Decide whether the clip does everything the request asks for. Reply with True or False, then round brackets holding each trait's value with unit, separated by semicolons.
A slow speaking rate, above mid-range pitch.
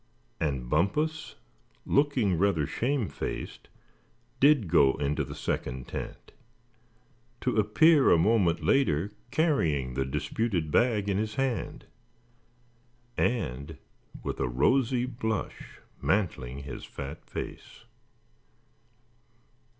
False (100 wpm; 100 Hz)